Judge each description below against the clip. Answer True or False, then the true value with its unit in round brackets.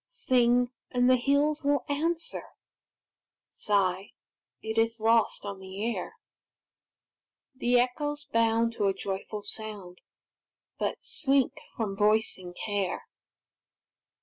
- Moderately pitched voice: False (230 Hz)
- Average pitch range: True (4.0 semitones)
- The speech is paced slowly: True (105 wpm)